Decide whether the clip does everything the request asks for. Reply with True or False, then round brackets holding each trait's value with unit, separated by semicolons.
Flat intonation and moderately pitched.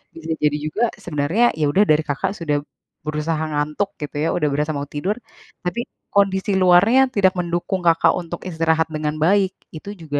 False (3.8 semitones; 165 Hz)